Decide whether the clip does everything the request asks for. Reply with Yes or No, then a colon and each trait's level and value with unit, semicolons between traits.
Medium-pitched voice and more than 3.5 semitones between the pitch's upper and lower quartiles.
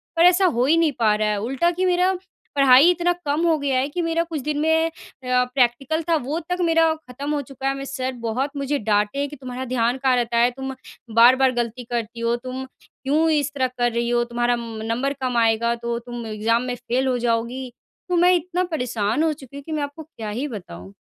No: very high, 260 Hz; average, 4.0 semitones